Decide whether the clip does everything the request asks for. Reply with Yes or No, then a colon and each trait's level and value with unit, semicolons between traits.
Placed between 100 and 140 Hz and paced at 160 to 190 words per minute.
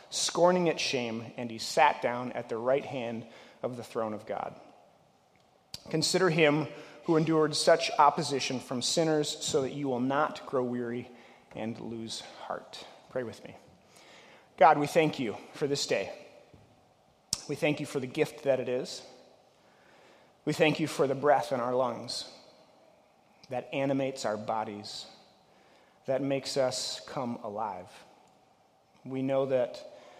No: low, 135 Hz; average, 145 wpm